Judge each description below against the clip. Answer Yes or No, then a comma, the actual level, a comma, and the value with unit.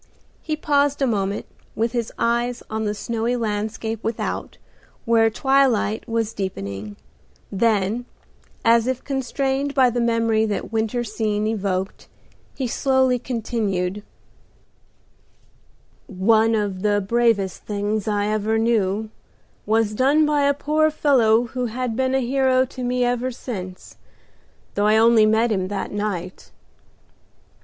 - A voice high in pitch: Yes, high, 225 Hz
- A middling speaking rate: No, slow, 130 wpm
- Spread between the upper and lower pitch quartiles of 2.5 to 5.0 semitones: Yes, average, 3.2 semitones